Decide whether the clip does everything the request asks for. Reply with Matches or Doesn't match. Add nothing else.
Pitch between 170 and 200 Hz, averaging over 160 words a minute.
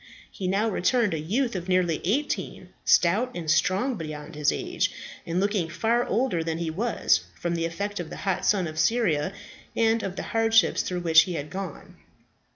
Matches